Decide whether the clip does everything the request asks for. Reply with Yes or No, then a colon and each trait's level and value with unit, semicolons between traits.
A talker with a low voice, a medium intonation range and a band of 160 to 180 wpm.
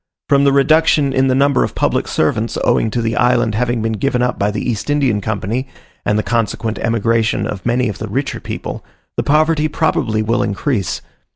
No: low, 120 Hz; average, 4.0 semitones; average, 195 wpm